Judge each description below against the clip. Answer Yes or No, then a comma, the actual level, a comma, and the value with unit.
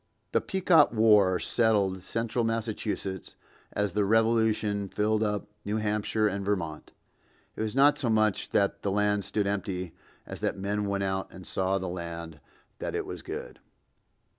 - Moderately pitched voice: No, low, 105 Hz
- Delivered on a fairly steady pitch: Yes, narrow, 2.3 semitones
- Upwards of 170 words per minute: No, average, 160 wpm